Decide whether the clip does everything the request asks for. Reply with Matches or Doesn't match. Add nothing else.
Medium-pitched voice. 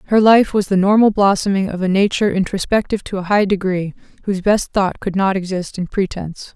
Doesn't match